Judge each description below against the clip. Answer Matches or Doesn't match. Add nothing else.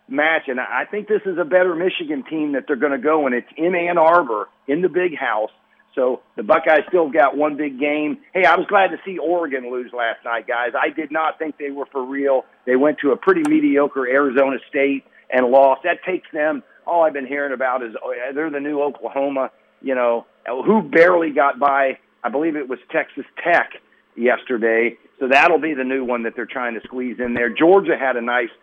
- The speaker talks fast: Matches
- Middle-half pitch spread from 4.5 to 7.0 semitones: Matches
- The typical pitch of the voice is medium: Matches